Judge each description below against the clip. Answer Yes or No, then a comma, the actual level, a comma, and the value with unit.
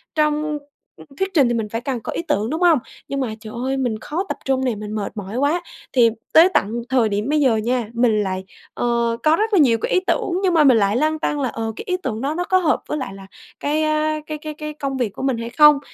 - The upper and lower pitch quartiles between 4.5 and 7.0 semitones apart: Yes, average, 5.1 semitones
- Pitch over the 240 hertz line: Yes, very high, 265 Hz